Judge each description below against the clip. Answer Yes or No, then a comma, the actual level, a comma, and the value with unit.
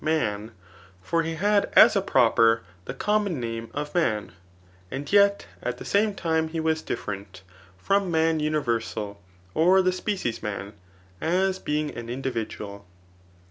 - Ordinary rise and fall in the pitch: No, wide, 8.2 semitones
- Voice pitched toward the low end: No, medium, 155 Hz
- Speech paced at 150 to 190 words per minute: No, average, 140 wpm